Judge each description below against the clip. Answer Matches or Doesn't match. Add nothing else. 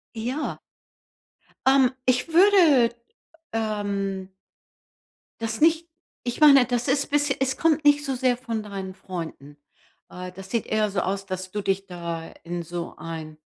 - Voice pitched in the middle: Doesn't match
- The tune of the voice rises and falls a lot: Matches